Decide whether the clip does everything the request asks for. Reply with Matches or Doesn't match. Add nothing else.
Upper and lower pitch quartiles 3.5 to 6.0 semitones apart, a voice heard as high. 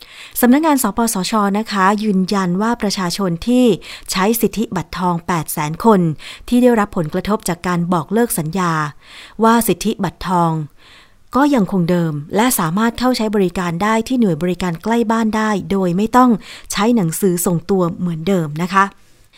Matches